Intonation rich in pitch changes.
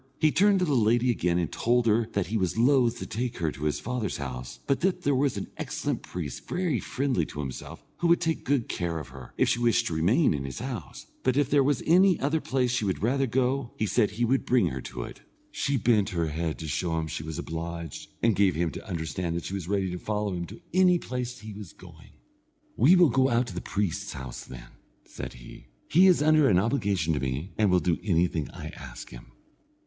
Yes: wide, 7.8 semitones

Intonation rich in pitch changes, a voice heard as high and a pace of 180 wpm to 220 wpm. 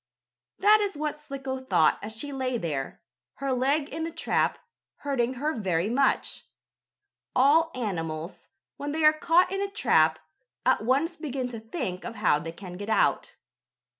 No: wide, 6.9 semitones; very high, 260 Hz; average, 165 wpm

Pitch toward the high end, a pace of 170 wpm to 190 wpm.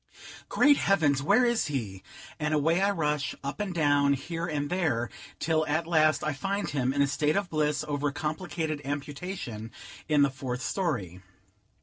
No: medium, 150 Hz; average, 175 wpm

